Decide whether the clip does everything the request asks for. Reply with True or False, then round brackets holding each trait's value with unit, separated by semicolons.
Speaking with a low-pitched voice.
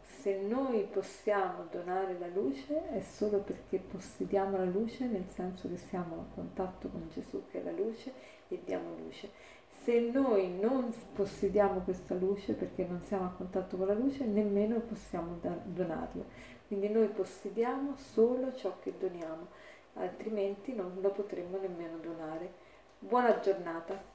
False (200 Hz)